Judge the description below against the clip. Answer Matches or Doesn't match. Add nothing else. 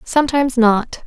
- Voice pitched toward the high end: Matches